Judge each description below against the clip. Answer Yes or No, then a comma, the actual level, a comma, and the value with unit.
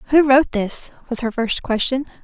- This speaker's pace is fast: No, average, 190 wpm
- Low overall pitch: No, very high, 250 Hz